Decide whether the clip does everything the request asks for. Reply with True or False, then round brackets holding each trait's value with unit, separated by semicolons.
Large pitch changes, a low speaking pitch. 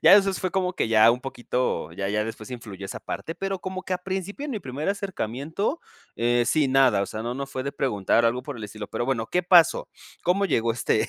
True (8.3 semitones; 130 Hz)